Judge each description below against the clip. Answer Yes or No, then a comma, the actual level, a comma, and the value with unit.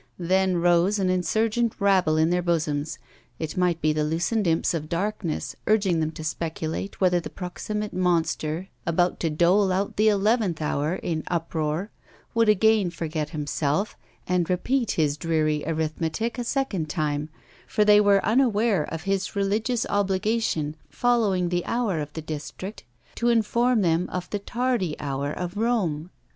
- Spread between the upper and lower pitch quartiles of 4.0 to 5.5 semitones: Yes, average, 4.8 semitones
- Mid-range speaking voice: Yes, medium, 180 Hz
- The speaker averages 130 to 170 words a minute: Yes, average, 155 wpm